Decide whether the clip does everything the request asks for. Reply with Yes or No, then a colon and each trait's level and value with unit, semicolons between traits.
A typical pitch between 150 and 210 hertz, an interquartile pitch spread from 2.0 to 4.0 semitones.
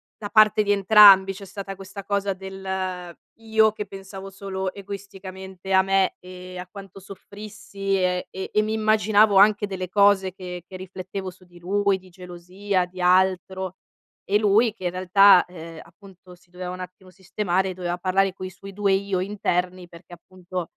No: high, 190 Hz; narrow, 1.6 semitones